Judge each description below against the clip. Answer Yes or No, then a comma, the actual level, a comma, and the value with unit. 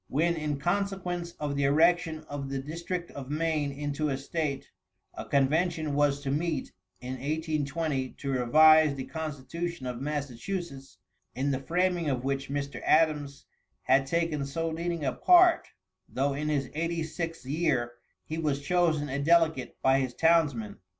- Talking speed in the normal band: Yes, average, 155 wpm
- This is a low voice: No, medium, 150 Hz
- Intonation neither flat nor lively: Yes, average, 3.2 semitones